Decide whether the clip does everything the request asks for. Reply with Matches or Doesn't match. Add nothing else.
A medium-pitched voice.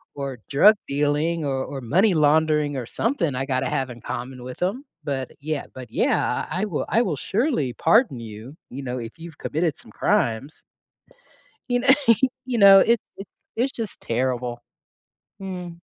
Matches